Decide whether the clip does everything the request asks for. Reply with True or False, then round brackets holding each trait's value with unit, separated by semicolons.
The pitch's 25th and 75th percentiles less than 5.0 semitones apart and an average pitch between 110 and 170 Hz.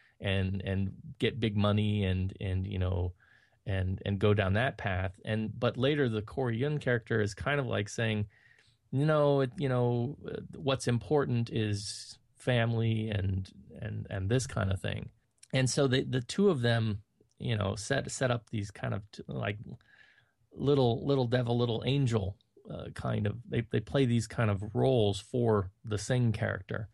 True (3.8 semitones; 115 Hz)